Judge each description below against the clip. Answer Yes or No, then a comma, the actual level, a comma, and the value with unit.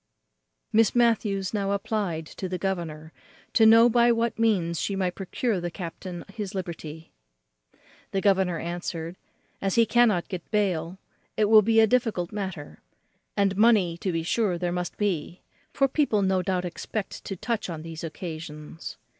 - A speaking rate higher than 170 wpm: No, average, 160 wpm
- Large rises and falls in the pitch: No, average, 4.0 semitones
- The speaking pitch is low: No, high, 190 Hz